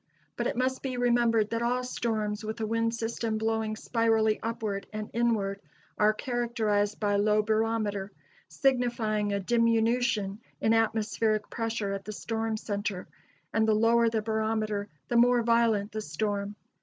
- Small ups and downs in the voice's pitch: Yes, narrow, 1.7 semitones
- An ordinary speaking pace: Yes, average, 150 wpm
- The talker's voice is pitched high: Yes, high, 220 Hz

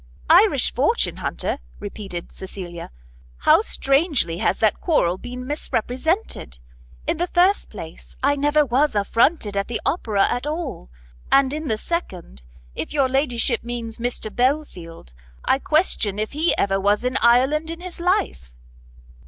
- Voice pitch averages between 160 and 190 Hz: No, high, 245 Hz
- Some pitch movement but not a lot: No, wide, 7.1 semitones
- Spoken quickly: No, average, 145 wpm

